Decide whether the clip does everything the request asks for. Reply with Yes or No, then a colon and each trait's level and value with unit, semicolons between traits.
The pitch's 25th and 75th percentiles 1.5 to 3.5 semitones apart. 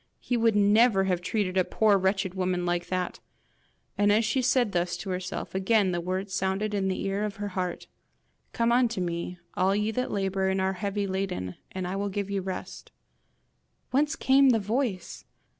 Yes: narrow, 2.5 semitones